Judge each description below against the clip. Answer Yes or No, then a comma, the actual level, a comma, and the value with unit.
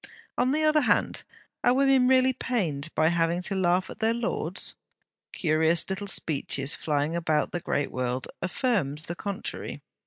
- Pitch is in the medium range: Yes, medium, 175 Hz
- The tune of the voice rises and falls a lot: Yes, wide, 7.9 semitones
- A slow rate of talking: No, average, 155 wpm